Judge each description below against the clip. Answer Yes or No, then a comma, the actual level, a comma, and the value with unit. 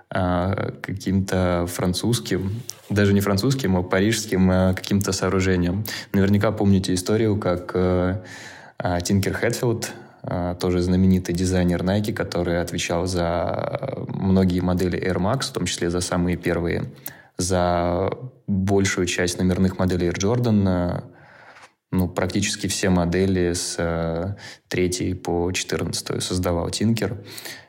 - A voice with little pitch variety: Yes, narrow, 2.2 semitones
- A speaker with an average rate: No, slow, 105 wpm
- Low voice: Yes, very low, 95 Hz